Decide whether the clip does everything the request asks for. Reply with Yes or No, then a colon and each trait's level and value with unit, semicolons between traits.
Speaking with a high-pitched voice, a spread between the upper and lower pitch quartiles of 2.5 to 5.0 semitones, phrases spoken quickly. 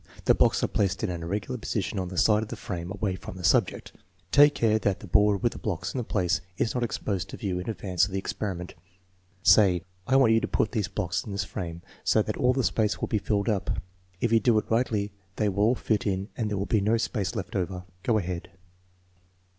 No: low, 105 Hz; average, 3.0 semitones; fast, 240 wpm